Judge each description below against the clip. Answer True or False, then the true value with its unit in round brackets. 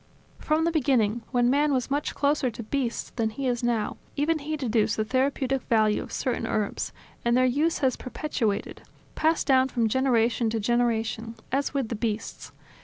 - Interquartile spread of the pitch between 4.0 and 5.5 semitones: False (3.6 semitones)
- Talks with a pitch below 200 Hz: False (245 Hz)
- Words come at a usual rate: True (180 wpm)